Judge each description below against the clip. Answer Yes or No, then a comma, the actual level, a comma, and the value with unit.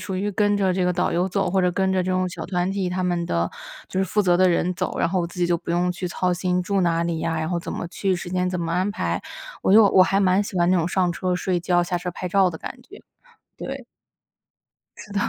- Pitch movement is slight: Yes, narrow, 1.4 semitones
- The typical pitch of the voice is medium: Yes, medium, 180 Hz